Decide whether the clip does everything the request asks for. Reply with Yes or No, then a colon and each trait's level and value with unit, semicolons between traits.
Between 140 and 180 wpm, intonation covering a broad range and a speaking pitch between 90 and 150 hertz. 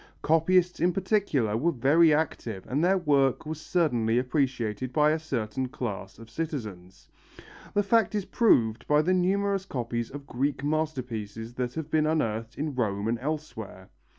Yes: average, 155 wpm; wide, 5.7 semitones; medium, 140 Hz